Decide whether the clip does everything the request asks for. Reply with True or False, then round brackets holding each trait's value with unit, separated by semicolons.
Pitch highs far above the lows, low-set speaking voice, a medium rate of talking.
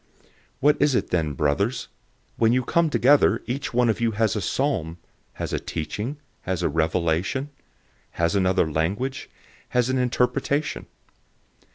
True (7.5 semitones; 115 Hz; 150 wpm)